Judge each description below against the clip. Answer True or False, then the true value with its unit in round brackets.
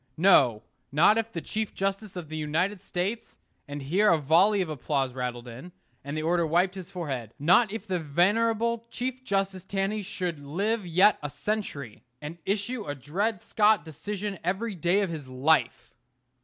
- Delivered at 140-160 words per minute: False (170 wpm)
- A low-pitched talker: False (180 Hz)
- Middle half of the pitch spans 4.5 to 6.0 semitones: True (5.6 semitones)